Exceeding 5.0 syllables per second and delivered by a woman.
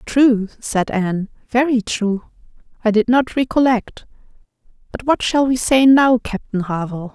No: 4.5 syllables/s; female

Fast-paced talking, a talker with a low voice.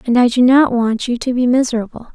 No: fast, 250 wpm; high, 245 Hz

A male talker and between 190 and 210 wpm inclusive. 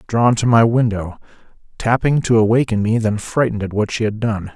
Yes: male; average, 200 wpm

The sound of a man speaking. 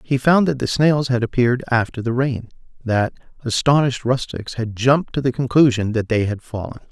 Yes: male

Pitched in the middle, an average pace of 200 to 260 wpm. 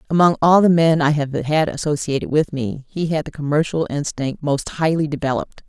No: medium, 150 Hz; average, 190 wpm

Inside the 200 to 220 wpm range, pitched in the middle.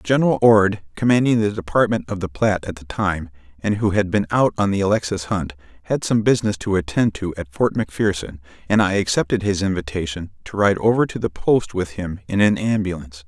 No: fast, 205 wpm; very low, 95 Hz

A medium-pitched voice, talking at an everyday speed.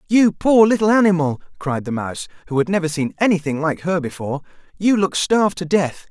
Yes: medium, 170 Hz; average, 195 wpm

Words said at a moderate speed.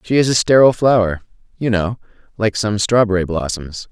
Yes: average, 155 wpm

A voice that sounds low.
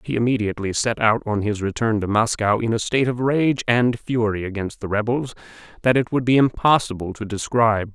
Yes: low, 115 Hz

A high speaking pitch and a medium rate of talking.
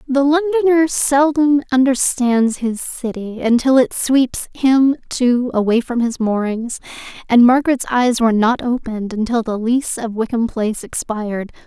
Yes: high, 245 Hz; average, 145 wpm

